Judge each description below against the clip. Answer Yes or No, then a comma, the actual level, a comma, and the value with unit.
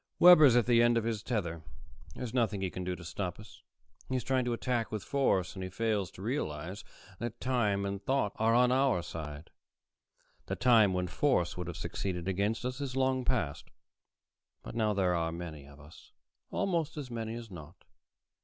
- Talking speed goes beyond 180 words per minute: Yes, average, 190 wpm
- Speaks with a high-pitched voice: No, low, 110 Hz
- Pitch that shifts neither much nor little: No, wide, 5.8 semitones